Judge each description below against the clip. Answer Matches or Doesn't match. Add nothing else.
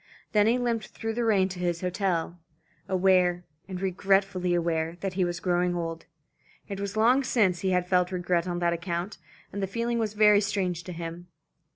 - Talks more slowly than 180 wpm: Doesn't match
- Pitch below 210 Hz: Matches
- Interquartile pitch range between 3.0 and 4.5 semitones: Doesn't match